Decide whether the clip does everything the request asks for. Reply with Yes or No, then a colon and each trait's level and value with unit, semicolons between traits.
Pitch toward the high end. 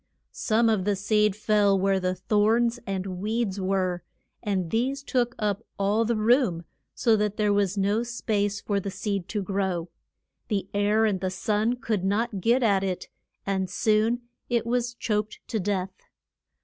Yes: high, 205 Hz